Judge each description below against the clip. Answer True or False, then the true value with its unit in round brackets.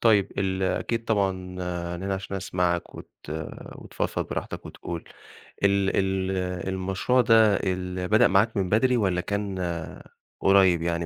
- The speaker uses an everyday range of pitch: False (2.0 semitones)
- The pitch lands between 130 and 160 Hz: False (95 Hz)